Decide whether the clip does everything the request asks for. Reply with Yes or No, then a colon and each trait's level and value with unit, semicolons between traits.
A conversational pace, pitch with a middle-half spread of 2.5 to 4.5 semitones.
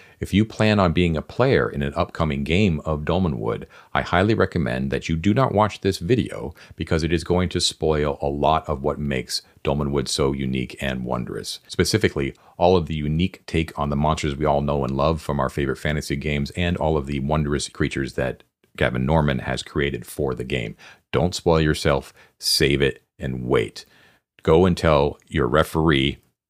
Yes: average, 190 wpm; average, 3.6 semitones